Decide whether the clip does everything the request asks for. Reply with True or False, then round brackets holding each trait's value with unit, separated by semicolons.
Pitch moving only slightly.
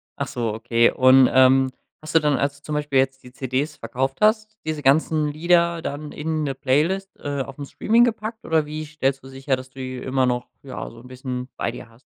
False (3.2 semitones)